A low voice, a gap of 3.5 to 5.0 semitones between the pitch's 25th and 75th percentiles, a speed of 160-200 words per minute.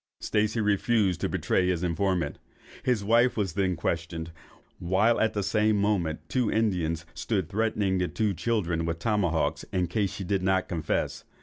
Yes: very low, 95 Hz; average, 3.9 semitones; average, 165 wpm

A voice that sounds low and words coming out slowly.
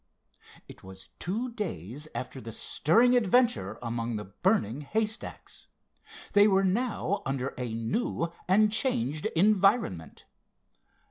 No: medium, 170 Hz; slow, 115 wpm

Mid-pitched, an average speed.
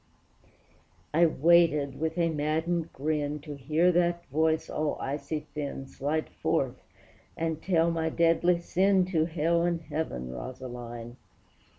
No: medium, 160 Hz; slow, 125 wpm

